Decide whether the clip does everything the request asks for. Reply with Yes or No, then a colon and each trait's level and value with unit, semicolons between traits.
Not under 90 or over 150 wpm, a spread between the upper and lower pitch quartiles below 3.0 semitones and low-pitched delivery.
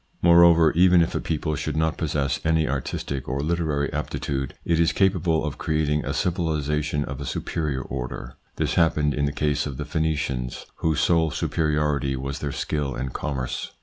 No: average, 175 wpm; narrow, 2.6 semitones; very low, 75 Hz